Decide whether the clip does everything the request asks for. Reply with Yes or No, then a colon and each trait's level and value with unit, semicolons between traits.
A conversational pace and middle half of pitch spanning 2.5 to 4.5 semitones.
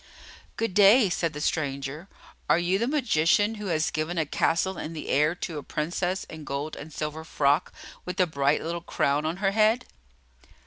Yes: average, 190 wpm; average, 4.0 semitones